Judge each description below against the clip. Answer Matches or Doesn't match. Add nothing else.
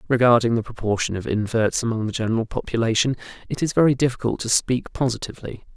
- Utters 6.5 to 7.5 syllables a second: Matches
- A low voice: Matches